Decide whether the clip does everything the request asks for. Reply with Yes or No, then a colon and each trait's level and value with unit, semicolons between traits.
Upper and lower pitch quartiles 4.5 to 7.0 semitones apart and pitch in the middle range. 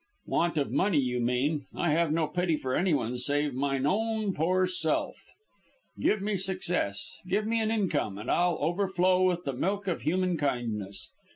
Yes: wide, 5.4 semitones; medium, 170 Hz